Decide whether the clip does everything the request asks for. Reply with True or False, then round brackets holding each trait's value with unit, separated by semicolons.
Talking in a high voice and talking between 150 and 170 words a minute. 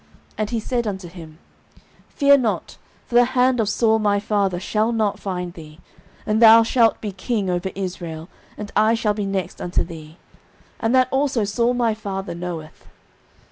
False (210 Hz; 180 wpm)